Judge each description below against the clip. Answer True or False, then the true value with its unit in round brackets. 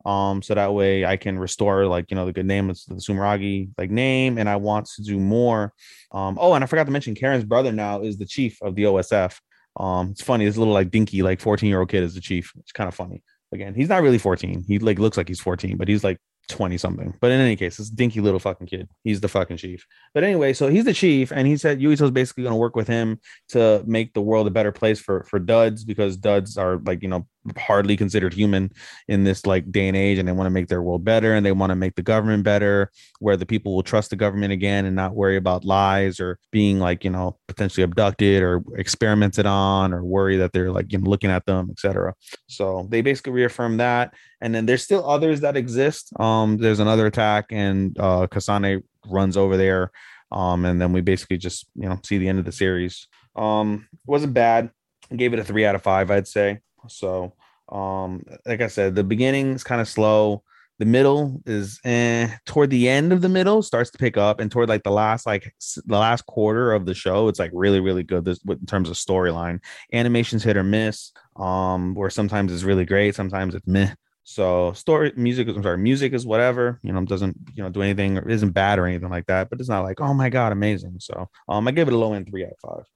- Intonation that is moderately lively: True (3.2 semitones)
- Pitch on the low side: True (100 Hz)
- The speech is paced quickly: True (240 wpm)